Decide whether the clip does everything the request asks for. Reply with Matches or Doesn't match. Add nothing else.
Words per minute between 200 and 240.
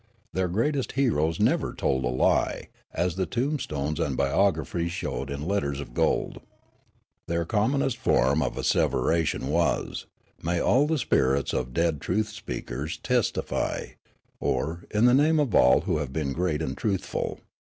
Doesn't match